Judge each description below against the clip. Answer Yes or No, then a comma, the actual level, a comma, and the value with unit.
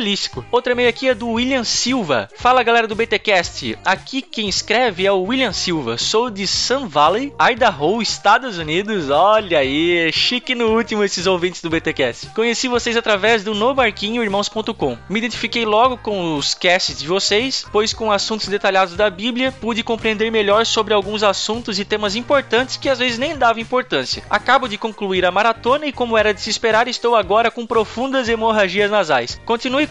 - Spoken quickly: No, average, 175 wpm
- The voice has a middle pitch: No, high, 220 Hz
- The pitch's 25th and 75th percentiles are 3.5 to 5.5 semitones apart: No, average, 3.1 semitones